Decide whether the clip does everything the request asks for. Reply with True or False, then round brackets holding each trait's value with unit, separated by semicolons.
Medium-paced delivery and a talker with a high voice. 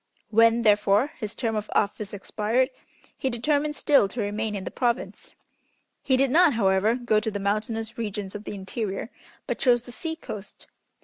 True (175 wpm; 220 Hz)